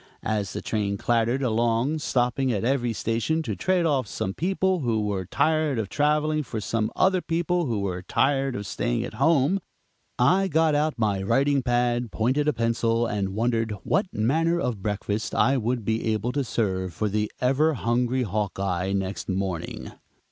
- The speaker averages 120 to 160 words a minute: No, average, 170 wpm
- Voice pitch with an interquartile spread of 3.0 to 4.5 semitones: No, wide, 5.4 semitones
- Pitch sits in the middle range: No, low, 120 Hz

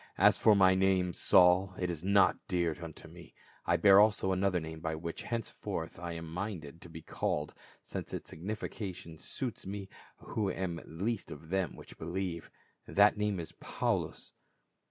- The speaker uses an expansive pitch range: No, average, 2.9 semitones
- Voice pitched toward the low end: Yes, very low, 90 Hz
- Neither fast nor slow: Yes, average, 165 wpm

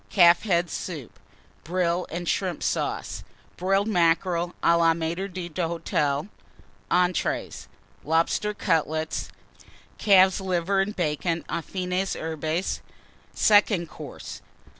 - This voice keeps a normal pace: No, slow, 100 wpm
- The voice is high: No, medium, 175 Hz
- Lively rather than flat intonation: No, narrow, 2.4 semitones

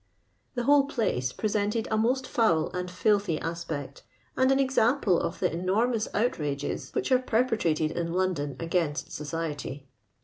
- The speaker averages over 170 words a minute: No, average, 140 wpm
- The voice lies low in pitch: No, medium, 185 Hz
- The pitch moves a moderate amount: No, wide, 6.8 semitones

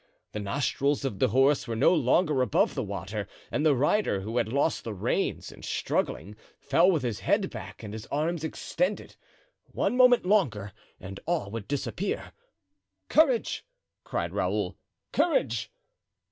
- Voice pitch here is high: No, medium, 140 Hz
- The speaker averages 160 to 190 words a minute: No, average, 145 wpm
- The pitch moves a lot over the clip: Yes, wide, 8.3 semitones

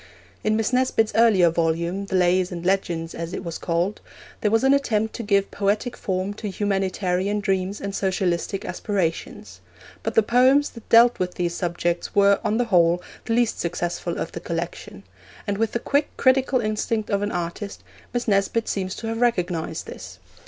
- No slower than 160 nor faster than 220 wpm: Yes, average, 180 wpm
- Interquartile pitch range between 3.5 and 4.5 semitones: Yes, average, 4.0 semitones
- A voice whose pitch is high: Yes, high, 200 Hz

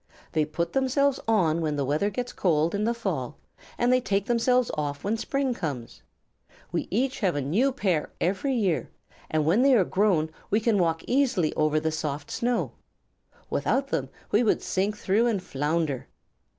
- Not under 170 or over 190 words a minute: Yes, average, 175 wpm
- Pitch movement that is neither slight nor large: No, wide, 7.4 semitones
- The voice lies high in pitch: Yes, high, 195 Hz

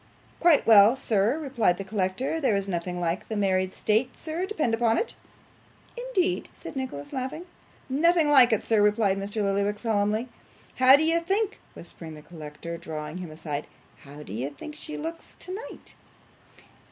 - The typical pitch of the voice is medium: No, high, 215 Hz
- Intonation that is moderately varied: No, wide, 8.3 semitones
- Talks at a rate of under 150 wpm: No, average, 165 wpm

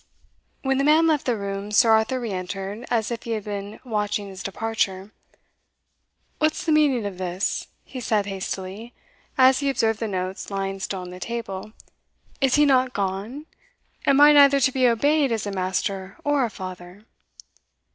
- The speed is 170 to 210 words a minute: Yes, average, 175 wpm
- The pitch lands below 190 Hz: No, high, 220 Hz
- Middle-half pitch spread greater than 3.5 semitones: Yes, average, 5.1 semitones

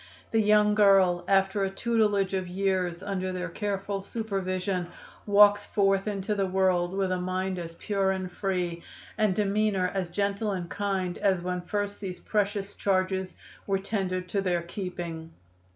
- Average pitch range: No, narrow, 1.8 semitones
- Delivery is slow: No, average, 155 wpm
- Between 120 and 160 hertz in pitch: No, high, 195 Hz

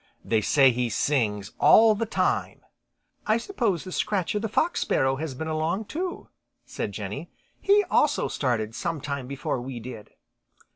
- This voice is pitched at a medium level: Yes, medium, 150 Hz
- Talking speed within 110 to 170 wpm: Yes, average, 145 wpm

